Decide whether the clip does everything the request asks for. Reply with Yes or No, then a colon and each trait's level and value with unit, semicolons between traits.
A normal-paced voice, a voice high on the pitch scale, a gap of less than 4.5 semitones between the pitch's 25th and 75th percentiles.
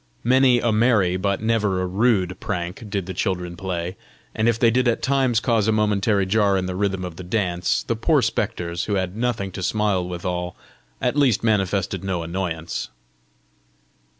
No: average, 180 wpm; low, 100 Hz; average, 3.8 semitones